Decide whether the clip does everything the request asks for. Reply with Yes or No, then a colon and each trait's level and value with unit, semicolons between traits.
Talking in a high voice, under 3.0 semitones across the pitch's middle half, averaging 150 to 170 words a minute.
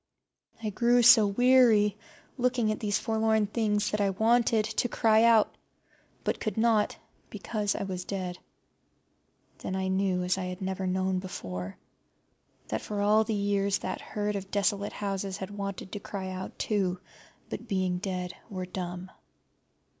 Yes: high, 200 Hz; narrow, 2.5 semitones; average, 155 wpm